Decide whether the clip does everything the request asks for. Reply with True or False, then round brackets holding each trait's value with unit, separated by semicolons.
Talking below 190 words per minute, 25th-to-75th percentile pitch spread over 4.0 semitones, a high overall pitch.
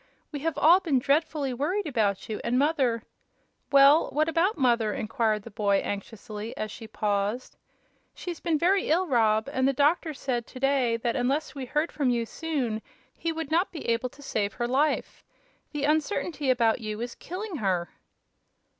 True (180 wpm; 5.5 semitones; 265 Hz)